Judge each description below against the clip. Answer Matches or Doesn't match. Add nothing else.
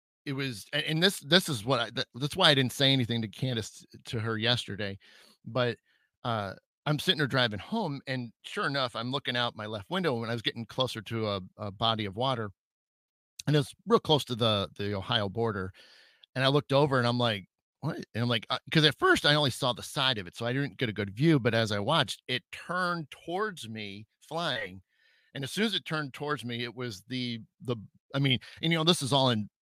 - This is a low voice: Matches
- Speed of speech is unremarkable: Doesn't match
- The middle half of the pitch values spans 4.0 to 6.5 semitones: Matches